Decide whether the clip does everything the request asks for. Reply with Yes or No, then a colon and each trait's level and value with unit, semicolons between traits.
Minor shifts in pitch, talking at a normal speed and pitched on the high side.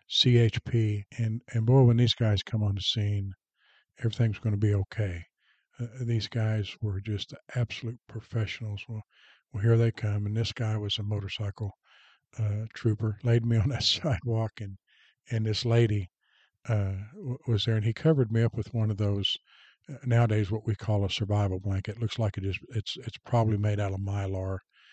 No: narrow, 2.1 semitones; average, 185 wpm; low, 110 Hz